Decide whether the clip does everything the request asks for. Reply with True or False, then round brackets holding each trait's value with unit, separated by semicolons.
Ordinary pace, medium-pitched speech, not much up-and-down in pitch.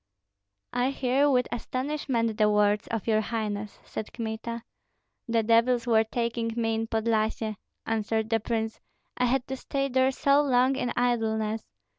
False (150 wpm; 230 Hz; 2.2 semitones)